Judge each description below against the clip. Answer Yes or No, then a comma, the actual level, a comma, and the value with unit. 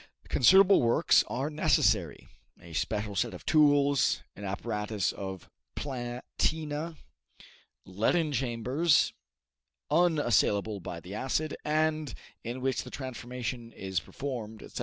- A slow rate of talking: Yes, slow, 110 wpm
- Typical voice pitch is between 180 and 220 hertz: No, low, 125 Hz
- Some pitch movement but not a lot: No, wide, 6.1 semitones